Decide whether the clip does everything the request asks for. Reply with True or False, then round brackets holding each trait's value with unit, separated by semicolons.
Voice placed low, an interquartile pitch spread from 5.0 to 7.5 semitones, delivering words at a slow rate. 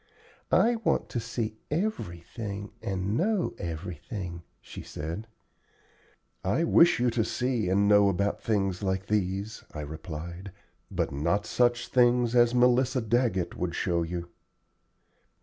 True (100 Hz; 5.3 semitones; 130 wpm)